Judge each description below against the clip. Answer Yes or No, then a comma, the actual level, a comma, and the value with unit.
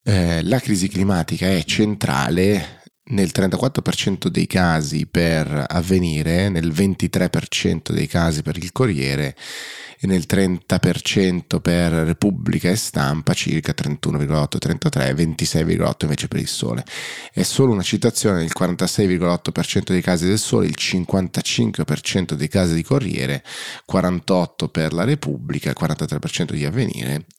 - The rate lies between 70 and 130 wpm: Yes, average, 125 wpm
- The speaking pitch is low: Yes, very low, 90 Hz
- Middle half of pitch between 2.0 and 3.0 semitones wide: No, average, 3.5 semitones